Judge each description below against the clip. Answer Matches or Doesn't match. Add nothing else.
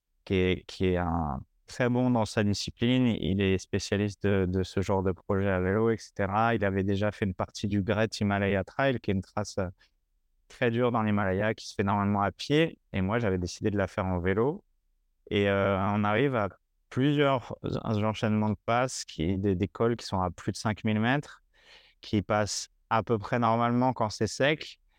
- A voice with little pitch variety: Doesn't match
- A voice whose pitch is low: Matches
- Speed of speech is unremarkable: Matches